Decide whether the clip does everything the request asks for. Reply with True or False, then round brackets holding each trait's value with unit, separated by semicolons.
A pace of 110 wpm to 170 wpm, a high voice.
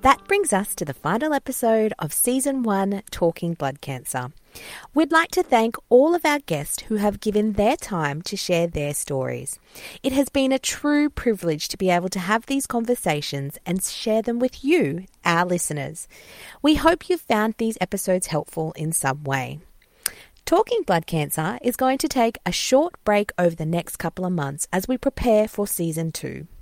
False (185 wpm; 205 Hz)